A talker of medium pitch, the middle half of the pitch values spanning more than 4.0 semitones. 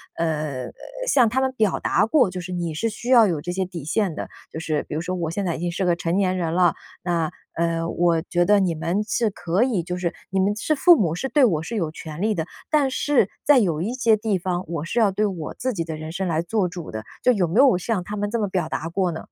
Yes: medium, 180 Hz; average, 4.4 semitones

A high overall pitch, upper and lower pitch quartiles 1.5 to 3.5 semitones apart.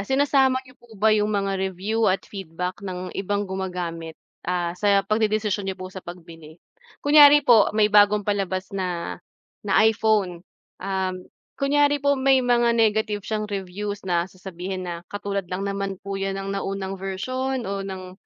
Yes: high, 195 Hz; average, 2.7 semitones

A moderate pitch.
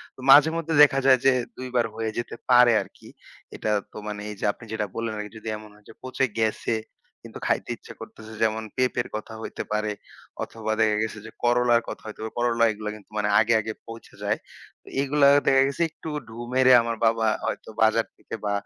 No: low, 115 Hz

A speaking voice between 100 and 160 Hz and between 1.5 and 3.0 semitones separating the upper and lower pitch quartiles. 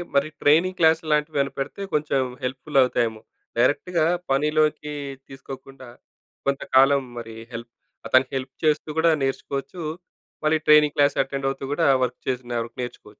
Yes: medium, 140 Hz; average, 2.7 semitones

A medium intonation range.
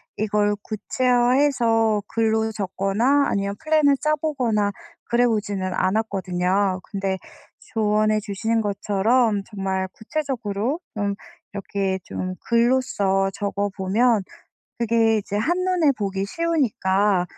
Yes: average, 3.6 semitones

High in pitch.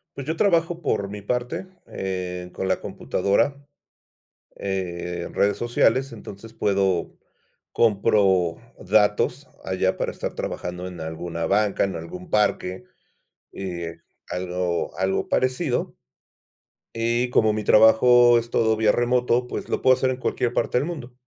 No: low, 105 Hz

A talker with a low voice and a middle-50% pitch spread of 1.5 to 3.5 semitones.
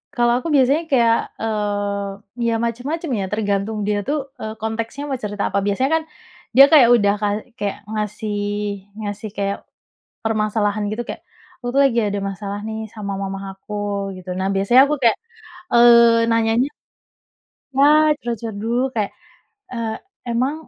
No: high, 220 Hz; average, 2.8 semitones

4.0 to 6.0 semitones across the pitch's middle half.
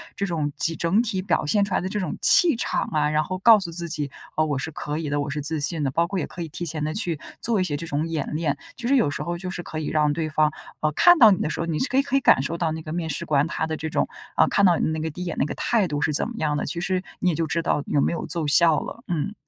No: average, 3.5 semitones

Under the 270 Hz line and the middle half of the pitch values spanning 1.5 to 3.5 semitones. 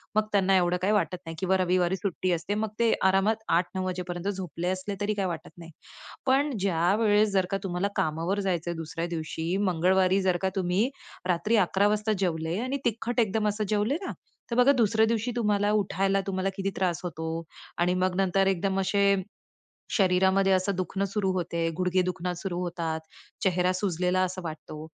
Yes: high, 190 Hz; narrow, 2.5 semitones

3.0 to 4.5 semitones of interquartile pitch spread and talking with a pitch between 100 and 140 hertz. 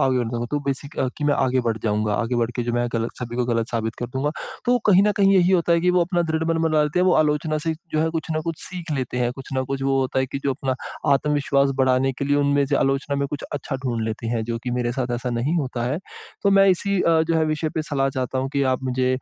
Yes: average, 4.1 semitones; low, 135 Hz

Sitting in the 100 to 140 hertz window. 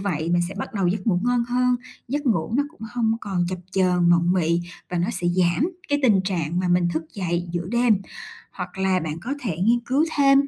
No: high, 190 Hz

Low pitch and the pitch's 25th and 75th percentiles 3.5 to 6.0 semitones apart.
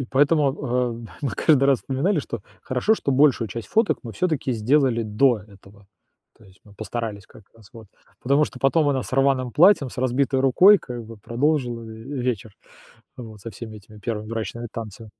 Yes: low, 120 Hz; average, 4.0 semitones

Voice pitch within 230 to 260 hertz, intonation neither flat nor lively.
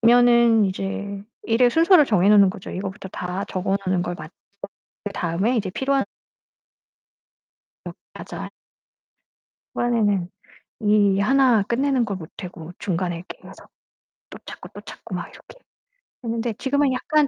No: high, 210 Hz; average, 4.4 semitones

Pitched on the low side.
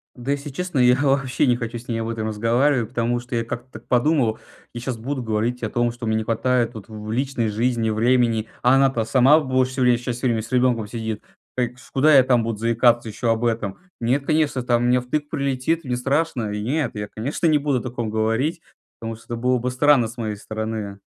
Yes: low, 120 Hz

